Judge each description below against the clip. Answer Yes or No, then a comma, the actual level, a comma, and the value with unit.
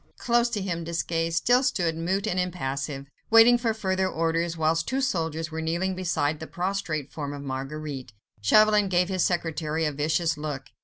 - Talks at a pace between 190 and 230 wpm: No, average, 170 wpm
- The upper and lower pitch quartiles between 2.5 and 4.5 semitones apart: Yes, average, 3.6 semitones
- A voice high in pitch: No, medium, 165 Hz